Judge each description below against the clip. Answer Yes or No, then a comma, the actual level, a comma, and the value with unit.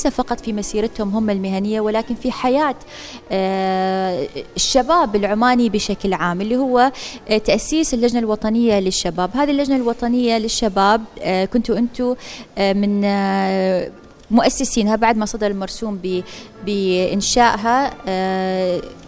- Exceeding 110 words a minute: No, average, 100 wpm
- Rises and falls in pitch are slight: No, average, 3.9 semitones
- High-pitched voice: Yes, high, 215 Hz